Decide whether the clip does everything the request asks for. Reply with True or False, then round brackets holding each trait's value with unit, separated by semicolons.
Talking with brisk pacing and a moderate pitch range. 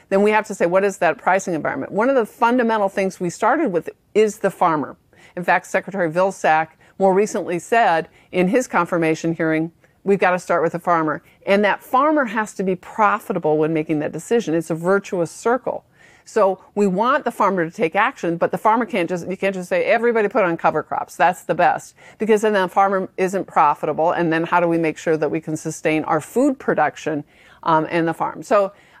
True (215 wpm; 4.0 semitones)